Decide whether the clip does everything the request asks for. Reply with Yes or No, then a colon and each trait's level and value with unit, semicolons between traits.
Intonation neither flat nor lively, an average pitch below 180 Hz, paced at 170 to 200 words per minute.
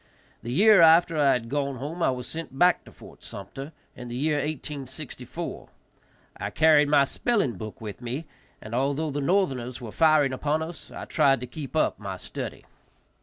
Yes: average, 4.0 semitones; medium, 140 Hz; average, 180 wpm